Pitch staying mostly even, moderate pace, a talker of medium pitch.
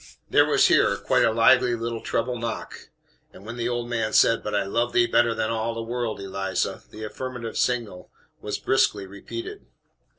No: narrow, 1.6 semitones; average, 185 wpm; low, 115 Hz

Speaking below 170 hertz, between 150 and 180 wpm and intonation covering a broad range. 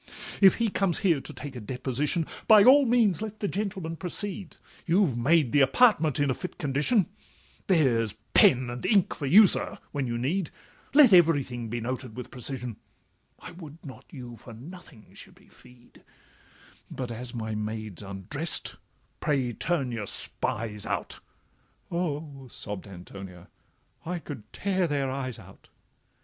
Yes: medium, 140 Hz; average, 160 wpm; wide, 6.9 semitones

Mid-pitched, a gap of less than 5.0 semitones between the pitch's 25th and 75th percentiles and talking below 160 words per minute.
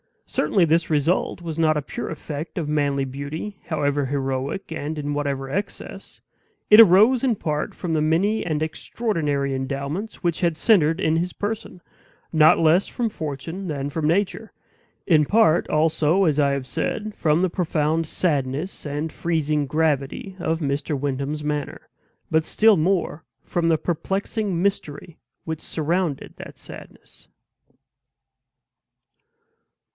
Yes: medium, 160 Hz; average, 3.6 semitones; average, 140 wpm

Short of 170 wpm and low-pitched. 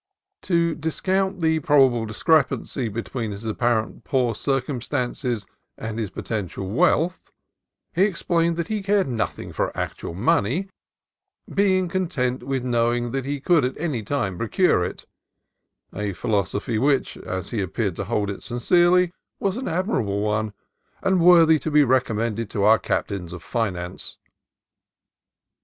Yes: average, 145 wpm; low, 125 Hz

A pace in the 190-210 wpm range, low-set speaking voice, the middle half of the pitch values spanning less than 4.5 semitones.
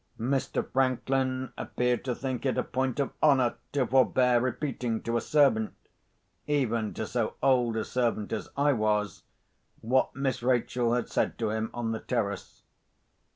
No: average, 150 wpm; low, 125 Hz; narrow, 2.5 semitones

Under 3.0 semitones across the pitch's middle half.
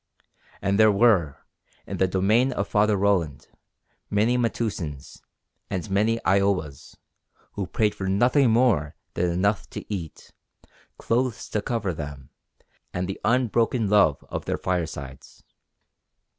No: average, 4.5 semitones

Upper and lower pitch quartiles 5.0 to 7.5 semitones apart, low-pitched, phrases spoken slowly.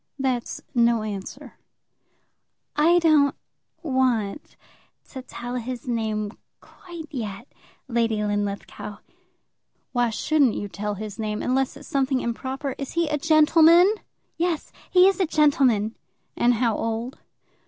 No: average, 5.3 semitones; very high, 255 Hz; slow, 120 wpm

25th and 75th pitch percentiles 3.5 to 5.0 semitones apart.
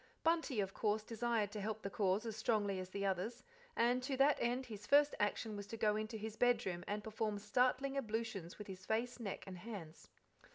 No: average, 2.9 semitones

